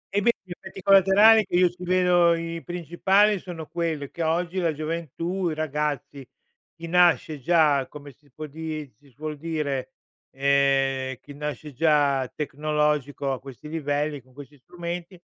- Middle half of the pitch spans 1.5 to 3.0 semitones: No, average, 3.4 semitones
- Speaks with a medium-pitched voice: Yes, medium, 155 Hz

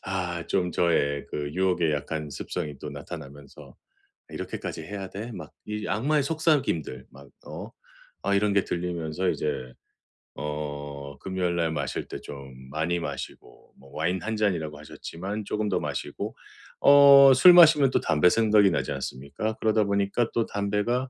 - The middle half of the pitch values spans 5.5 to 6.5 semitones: Yes, wide, 6.2 semitones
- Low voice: Yes, very low, 90 Hz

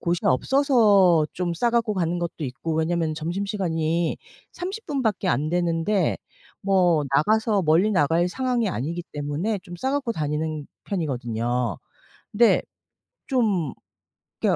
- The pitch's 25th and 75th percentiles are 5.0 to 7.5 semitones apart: Yes, average, 5.3 semitones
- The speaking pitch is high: No, medium, 175 Hz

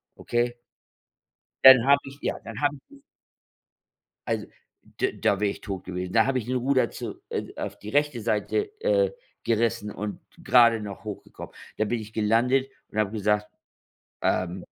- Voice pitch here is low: Yes, low, 115 Hz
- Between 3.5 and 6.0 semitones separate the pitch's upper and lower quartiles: Yes, average, 3.9 semitones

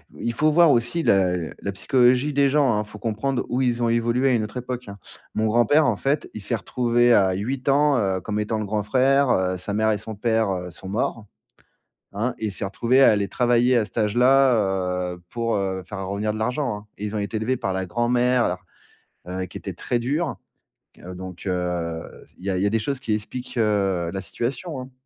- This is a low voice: Yes, low, 110 Hz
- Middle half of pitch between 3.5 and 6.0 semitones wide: Yes, average, 4.2 semitones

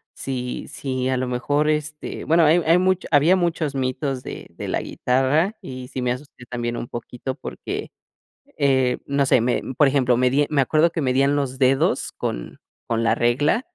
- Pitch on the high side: No, low, 135 Hz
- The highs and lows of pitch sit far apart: No, average, 3.2 semitones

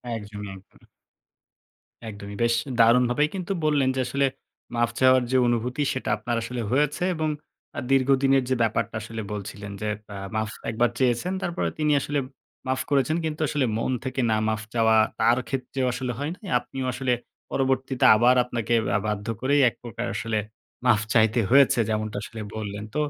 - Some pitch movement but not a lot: Yes, average, 3.5 semitones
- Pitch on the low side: Yes, low, 125 Hz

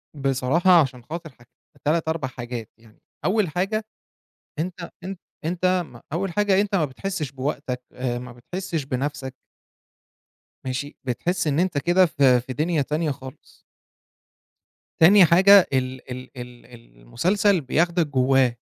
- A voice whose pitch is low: No, medium, 150 Hz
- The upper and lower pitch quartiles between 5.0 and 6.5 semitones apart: Yes, wide, 5.6 semitones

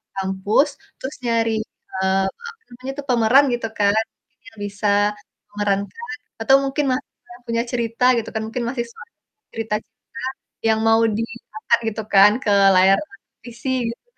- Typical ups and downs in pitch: Yes, average, 3.7 semitones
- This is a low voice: No, high, 230 Hz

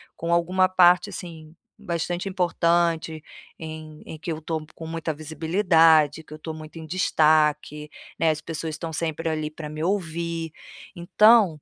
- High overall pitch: No, medium, 160 Hz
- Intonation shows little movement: Yes, narrow, 1.7 semitones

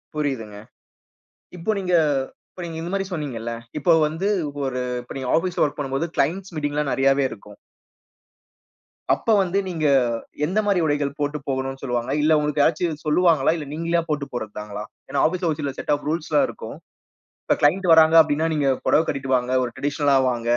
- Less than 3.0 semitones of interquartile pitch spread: No, average, 3.7 semitones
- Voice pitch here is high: No, medium, 150 Hz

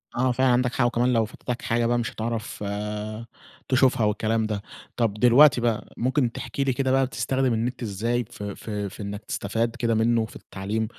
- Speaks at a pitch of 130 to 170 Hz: No, low, 115 Hz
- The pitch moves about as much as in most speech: No, narrow, 2.2 semitones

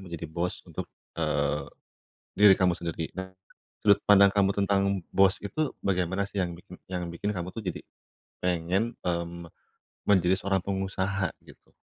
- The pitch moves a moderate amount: No, narrow, 2.2 semitones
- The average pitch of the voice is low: Yes, very low, 95 Hz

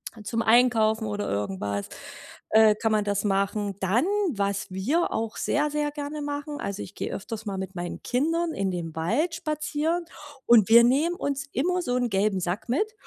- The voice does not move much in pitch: No, wide, 6.7 semitones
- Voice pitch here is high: Yes, high, 225 Hz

